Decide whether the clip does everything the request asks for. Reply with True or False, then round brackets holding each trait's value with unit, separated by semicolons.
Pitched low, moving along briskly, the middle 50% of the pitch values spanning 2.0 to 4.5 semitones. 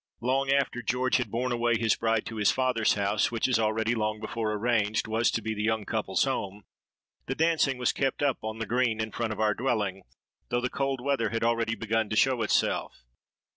True (115 Hz; 210 wpm; 2.6 semitones)